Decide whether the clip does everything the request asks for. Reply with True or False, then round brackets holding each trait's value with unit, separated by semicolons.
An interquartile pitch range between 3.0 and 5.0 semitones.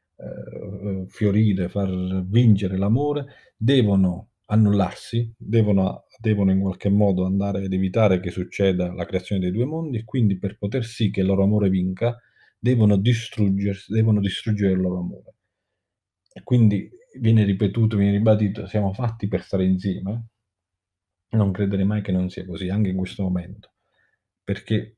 False (2.5 semitones)